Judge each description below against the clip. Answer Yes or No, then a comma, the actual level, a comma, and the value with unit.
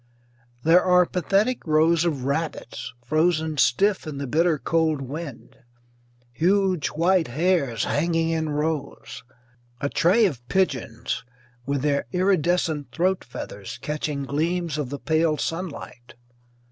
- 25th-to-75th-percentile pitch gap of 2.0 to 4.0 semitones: Yes, average, 3.7 semitones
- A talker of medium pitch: Yes, medium, 160 Hz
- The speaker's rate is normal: No, slow, 120 wpm